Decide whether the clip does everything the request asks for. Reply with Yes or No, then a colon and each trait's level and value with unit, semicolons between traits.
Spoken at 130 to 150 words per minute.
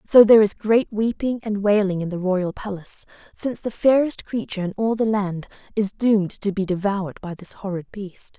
No: average, 200 wpm